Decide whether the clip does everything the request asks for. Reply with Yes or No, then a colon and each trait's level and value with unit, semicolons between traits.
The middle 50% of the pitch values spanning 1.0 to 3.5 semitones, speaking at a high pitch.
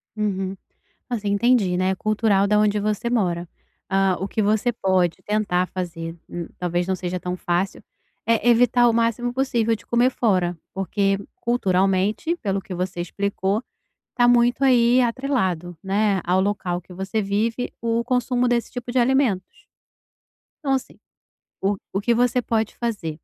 No: average, 4.2 semitones; high, 205 Hz